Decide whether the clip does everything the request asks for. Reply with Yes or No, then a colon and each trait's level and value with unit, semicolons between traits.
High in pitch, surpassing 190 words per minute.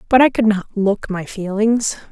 Yes: high, 210 Hz; average, 200 wpm